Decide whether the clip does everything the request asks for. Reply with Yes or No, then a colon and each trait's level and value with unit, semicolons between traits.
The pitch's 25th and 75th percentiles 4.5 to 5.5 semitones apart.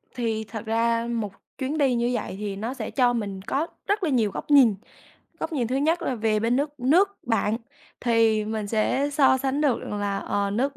No: average, 4.1 semitones